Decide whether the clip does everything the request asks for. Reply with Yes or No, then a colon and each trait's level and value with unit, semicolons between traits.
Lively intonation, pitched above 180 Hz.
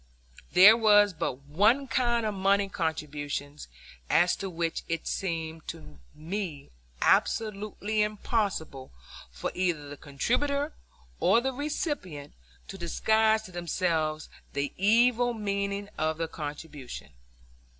Yes: wide, 5.7 semitones; high, 190 Hz